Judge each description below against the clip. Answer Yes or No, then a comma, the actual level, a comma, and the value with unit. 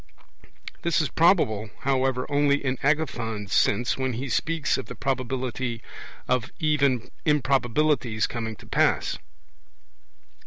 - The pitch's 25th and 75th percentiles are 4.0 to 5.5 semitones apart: No, average, 3.5 semitones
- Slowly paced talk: Yes, slow, 115 wpm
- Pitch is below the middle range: Yes, low, 130 Hz